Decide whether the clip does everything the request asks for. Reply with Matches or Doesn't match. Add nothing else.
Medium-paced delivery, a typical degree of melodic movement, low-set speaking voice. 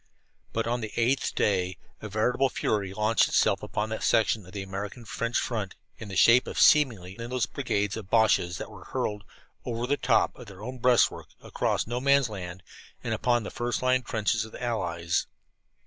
Matches